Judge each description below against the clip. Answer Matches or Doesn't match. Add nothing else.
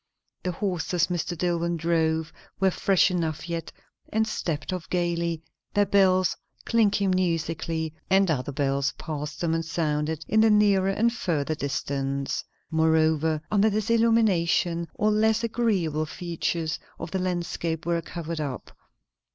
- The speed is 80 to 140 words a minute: Matches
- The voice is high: Doesn't match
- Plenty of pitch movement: Doesn't match